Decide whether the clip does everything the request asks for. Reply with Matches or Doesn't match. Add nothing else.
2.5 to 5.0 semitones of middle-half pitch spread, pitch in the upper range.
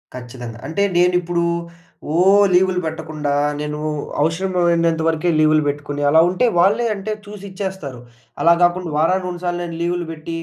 Doesn't match